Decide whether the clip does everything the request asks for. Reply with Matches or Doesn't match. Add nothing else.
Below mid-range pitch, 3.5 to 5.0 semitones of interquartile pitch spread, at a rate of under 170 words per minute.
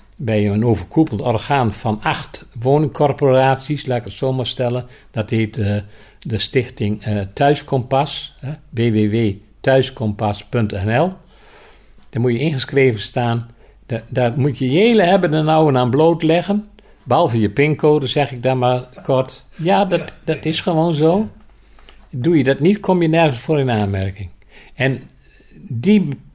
Doesn't match